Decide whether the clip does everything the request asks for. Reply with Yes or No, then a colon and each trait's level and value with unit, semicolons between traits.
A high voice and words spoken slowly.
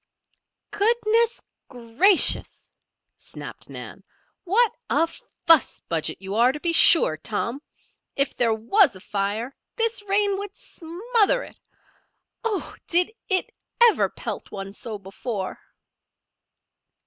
Yes: very high, 325 Hz; slow, 115 wpm